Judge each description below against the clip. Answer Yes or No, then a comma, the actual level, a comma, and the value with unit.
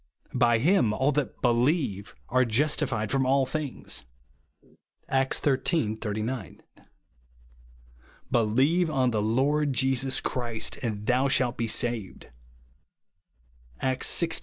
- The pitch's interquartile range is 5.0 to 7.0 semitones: No, average, 3.7 semitones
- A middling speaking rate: No, slow, 110 wpm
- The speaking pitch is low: Yes, low, 125 Hz